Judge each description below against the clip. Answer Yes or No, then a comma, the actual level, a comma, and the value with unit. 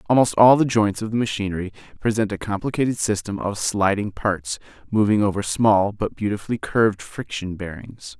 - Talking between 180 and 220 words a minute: No, average, 160 wpm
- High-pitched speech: No, low, 105 Hz